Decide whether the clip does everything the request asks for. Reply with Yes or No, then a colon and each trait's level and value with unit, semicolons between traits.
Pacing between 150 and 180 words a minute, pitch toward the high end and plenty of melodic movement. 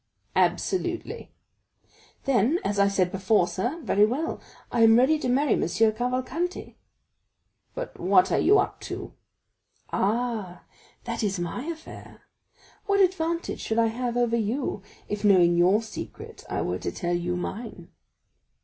No: average, 140 wpm; high, 225 Hz; wide, 6.4 semitones